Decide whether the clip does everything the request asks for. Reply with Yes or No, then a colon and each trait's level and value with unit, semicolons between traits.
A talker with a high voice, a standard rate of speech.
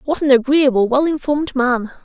Yes: very high, 270 Hz; average, 175 wpm